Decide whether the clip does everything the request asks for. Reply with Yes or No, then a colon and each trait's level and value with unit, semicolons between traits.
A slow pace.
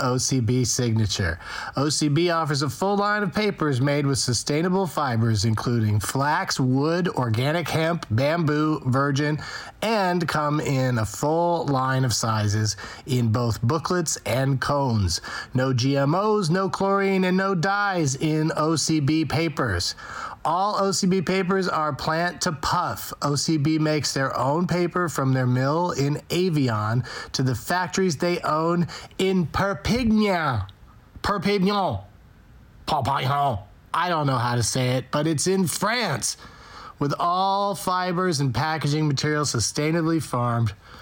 Yes: slow, 130 wpm